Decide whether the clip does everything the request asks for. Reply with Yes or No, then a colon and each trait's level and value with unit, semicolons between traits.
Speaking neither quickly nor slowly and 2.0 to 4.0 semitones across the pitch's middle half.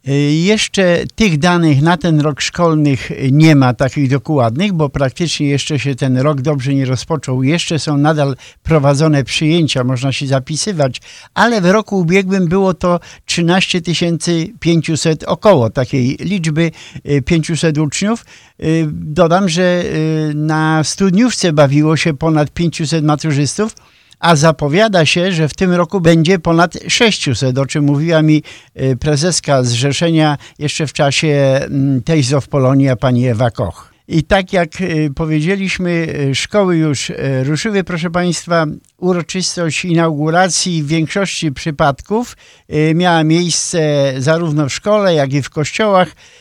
Yes: average, 125 wpm; average, 3.6 semitones